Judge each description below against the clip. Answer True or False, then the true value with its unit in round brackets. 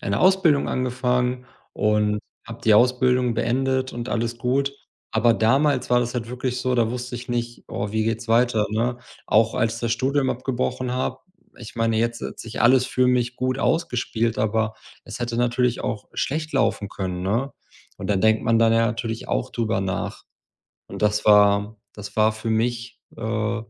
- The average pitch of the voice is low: True (120 Hz)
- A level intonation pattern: True (2.2 semitones)